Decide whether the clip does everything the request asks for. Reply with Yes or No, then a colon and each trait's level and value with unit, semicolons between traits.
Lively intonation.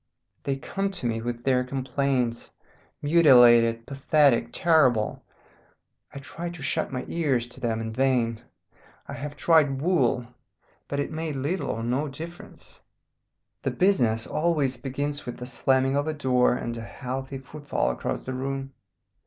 No: average, 3.2 semitones